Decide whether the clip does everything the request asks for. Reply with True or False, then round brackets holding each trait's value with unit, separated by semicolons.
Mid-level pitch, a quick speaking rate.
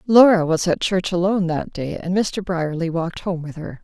True (175 Hz; 220 wpm)